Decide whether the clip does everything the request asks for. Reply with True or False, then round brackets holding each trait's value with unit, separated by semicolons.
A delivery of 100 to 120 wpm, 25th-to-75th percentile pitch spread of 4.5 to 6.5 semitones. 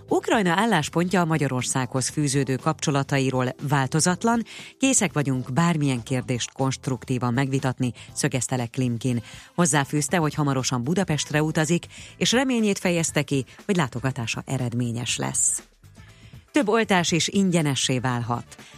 True (110 wpm; 5.1 semitones)